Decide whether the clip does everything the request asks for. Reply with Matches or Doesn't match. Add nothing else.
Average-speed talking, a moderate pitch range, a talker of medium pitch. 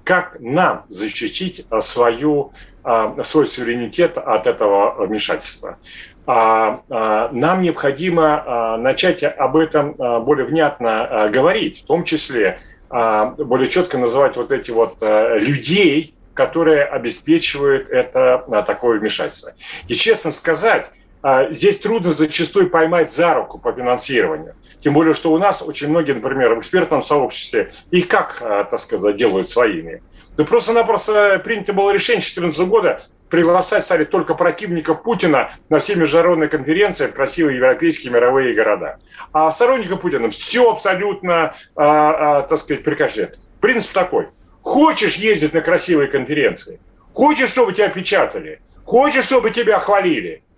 Doesn't match